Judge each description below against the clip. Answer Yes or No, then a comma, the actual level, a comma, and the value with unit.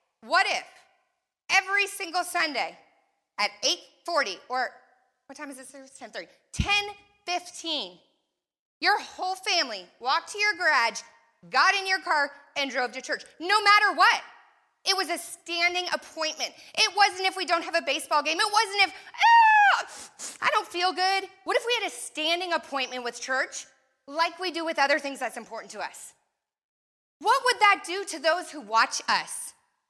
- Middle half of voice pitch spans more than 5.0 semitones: Yes, wide, 5.4 semitones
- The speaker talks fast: No, average, 165 wpm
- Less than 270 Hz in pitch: No, very high, 350 Hz